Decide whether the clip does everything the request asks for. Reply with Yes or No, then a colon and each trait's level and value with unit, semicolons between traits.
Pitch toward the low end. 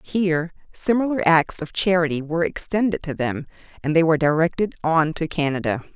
No: medium, 165 Hz